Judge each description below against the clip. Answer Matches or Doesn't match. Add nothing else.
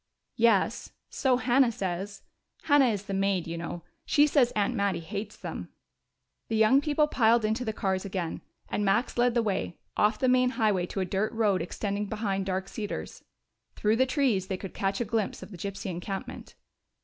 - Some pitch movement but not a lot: Matches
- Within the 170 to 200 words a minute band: Matches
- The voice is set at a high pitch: Matches